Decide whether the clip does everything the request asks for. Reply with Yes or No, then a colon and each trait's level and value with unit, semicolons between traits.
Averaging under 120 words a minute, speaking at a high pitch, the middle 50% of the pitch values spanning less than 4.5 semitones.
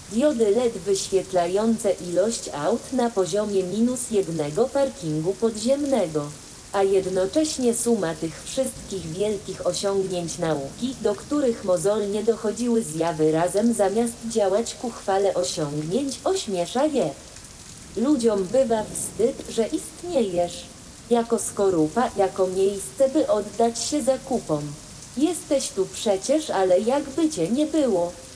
No: slow, 110 wpm; high, 205 Hz; average, 4.9 semitones